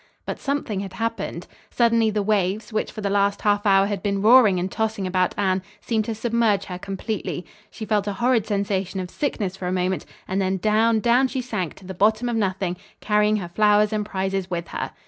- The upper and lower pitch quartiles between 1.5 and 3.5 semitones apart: Yes, narrow, 2.5 semitones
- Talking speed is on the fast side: Yes, fast, 210 wpm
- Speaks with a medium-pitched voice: No, high, 205 Hz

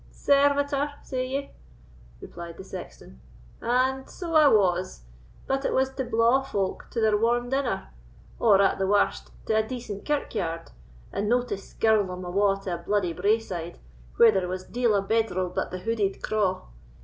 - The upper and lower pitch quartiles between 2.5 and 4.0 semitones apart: No, average, 5.2 semitones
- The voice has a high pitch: Yes, high, 215 Hz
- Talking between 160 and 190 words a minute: Yes, average, 170 wpm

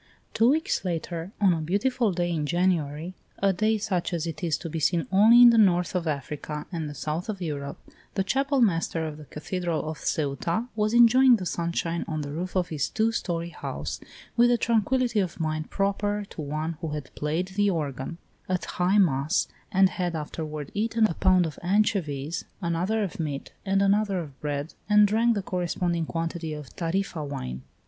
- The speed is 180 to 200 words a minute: Yes, average, 190 wpm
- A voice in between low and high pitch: Yes, medium, 175 Hz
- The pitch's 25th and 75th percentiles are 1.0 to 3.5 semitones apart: No, average, 4.7 semitones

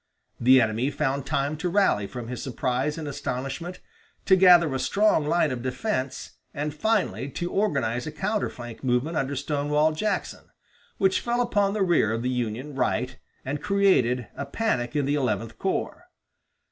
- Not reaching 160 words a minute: No, average, 165 wpm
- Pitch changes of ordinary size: No, wide, 5.9 semitones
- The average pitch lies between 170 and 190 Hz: No, medium, 145 Hz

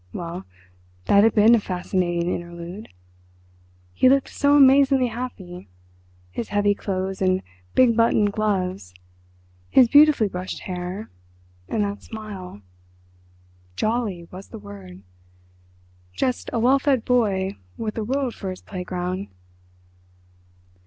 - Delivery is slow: Yes, slow, 115 wpm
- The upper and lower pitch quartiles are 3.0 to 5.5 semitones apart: Yes, average, 4.5 semitones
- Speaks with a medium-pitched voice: No, high, 195 Hz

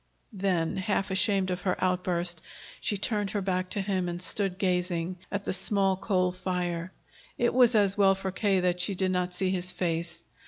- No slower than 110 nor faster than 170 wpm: No, average, 190 wpm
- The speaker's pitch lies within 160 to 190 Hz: Yes, medium, 185 Hz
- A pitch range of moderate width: No, narrow, 1.6 semitones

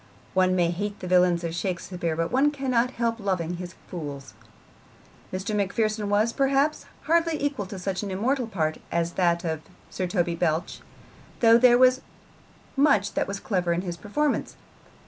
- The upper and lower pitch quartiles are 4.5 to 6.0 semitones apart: Yes, wide, 5.4 semitones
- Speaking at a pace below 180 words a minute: Yes, average, 165 wpm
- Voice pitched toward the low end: No, high, 195 Hz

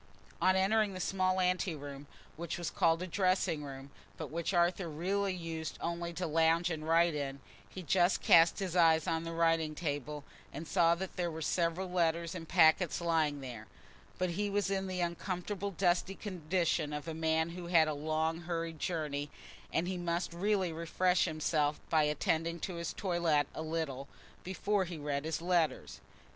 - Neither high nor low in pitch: Yes, medium, 170 Hz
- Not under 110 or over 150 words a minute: No, average, 180 wpm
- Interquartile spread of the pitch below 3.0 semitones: Yes, narrow, 2.5 semitones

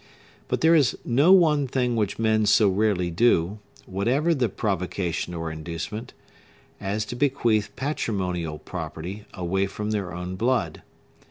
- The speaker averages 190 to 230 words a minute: No, average, 140 wpm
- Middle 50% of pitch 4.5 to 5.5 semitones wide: Yes, average, 5.2 semitones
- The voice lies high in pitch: No, low, 105 Hz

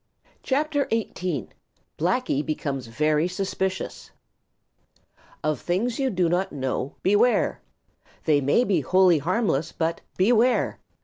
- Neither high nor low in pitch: Yes, medium, 180 Hz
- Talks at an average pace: No, slow, 110 wpm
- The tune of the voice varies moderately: No, wide, 6.6 semitones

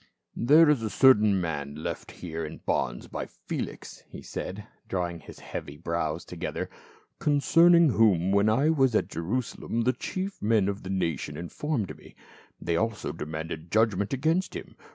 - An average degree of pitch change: No, wide, 7.5 semitones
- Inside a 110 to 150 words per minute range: No, average, 170 wpm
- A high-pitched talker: No, low, 100 Hz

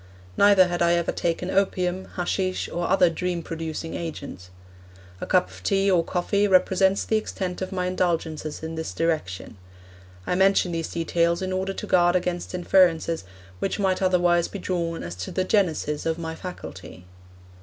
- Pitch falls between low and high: Yes, medium, 175 Hz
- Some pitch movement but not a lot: No, narrow, 2.2 semitones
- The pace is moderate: Yes, average, 165 wpm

